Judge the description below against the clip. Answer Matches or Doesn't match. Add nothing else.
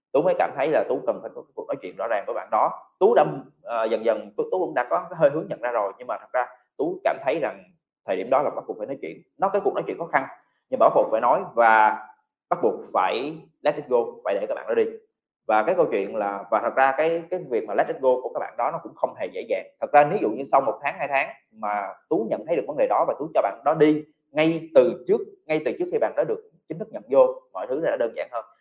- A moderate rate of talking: Doesn't match